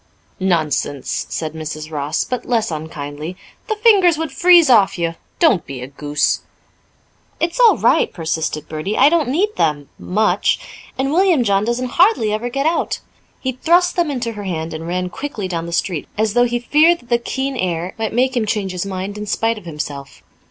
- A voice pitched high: Yes, high, 210 Hz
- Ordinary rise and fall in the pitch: No, wide, 8.9 semitones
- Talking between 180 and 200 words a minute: Yes, average, 190 wpm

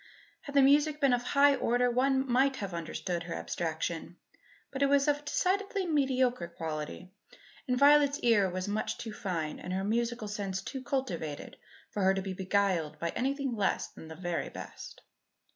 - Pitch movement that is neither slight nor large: No, wide, 7.1 semitones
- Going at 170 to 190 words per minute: Yes, average, 180 wpm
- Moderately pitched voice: No, high, 230 Hz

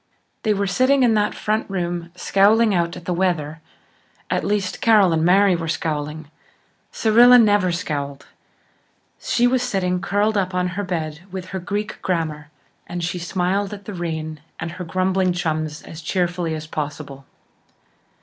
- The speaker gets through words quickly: No, average, 160 wpm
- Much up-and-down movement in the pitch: No, average, 3.9 semitones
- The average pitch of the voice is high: No, medium, 180 Hz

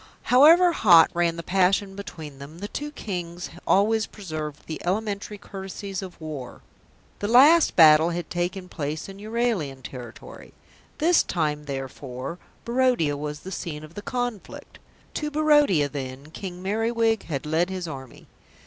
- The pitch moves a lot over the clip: Yes, wide, 6.1 semitones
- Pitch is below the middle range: No, medium, 180 Hz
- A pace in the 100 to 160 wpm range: Yes, average, 145 wpm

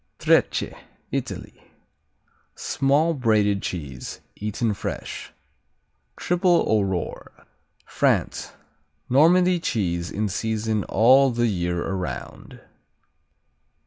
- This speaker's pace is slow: Yes, slow, 80 wpm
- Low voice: Yes, low, 110 Hz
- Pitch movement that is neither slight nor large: No, wide, 6.0 semitones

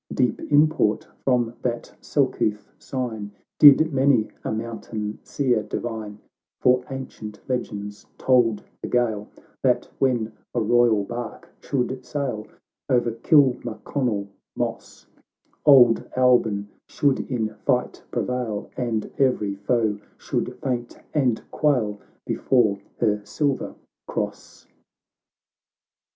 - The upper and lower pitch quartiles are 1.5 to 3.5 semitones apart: Yes, average, 3.1 semitones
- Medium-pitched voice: No, low, 120 Hz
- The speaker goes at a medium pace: No, slow, 105 wpm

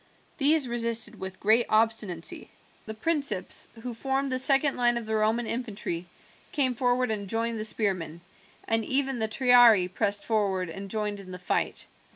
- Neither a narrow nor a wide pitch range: Yes, average, 3.6 semitones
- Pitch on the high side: Yes, high, 225 Hz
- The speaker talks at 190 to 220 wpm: No, average, 165 wpm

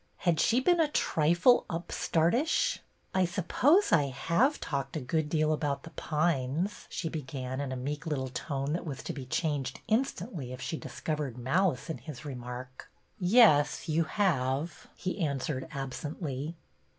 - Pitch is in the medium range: Yes, medium, 155 Hz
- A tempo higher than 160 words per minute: No, average, 155 wpm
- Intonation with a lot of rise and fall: No, average, 4.3 semitones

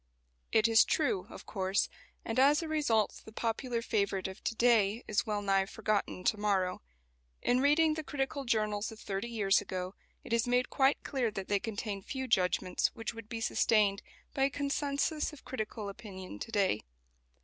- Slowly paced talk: No, average, 180 wpm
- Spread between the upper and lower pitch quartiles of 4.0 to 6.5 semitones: Yes, average, 4.4 semitones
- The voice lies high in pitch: Yes, high, 220 Hz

